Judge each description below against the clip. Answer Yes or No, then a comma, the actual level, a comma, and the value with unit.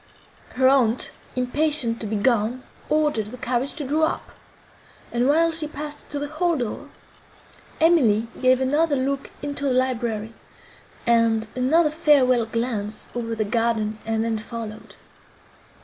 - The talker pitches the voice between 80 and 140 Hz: No, very high, 255 Hz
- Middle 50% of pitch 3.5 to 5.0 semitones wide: Yes, average, 4.4 semitones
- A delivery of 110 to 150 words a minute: Yes, average, 140 wpm